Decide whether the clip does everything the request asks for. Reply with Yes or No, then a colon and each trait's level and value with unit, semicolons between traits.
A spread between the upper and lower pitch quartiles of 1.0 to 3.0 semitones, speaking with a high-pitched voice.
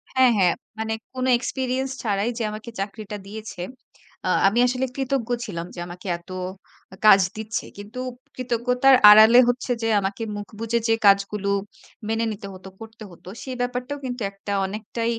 No: average, 3.7 semitones; high, 220 Hz